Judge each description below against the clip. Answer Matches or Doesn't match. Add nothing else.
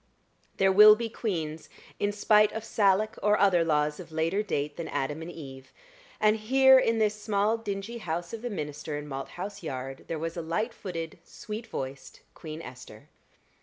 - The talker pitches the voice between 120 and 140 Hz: Doesn't match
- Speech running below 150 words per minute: Doesn't match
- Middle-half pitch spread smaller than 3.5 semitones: Doesn't match